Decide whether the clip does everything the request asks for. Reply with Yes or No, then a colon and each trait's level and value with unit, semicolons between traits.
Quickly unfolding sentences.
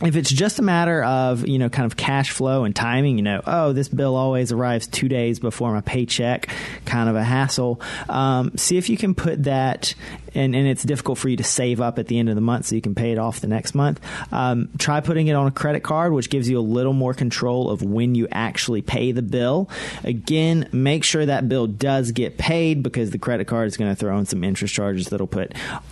Yes: fast, 245 wpm